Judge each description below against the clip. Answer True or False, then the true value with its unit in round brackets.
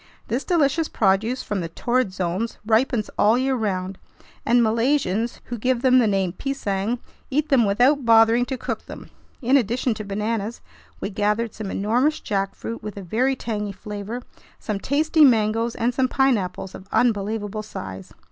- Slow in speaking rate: False (160 wpm)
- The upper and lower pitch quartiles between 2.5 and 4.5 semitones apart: True (3.8 semitones)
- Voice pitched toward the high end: True (225 Hz)